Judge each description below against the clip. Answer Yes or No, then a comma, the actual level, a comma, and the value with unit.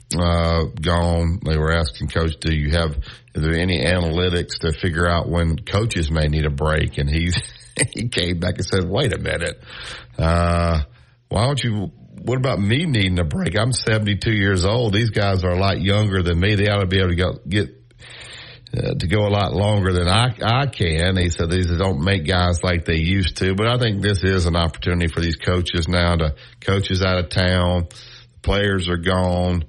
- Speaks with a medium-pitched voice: No, very low, 90 Hz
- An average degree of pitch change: Yes, average, 3.3 semitones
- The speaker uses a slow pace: No, fast, 205 wpm